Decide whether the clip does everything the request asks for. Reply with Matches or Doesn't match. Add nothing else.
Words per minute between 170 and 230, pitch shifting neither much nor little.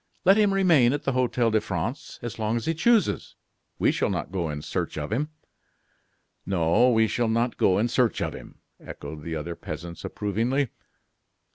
Doesn't match